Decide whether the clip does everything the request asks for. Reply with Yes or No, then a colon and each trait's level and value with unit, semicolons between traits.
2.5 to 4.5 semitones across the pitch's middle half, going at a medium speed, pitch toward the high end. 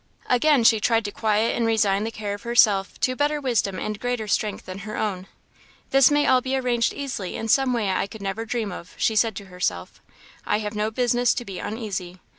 No: average, 3.4 semitones; fast, 220 wpm; high, 220 Hz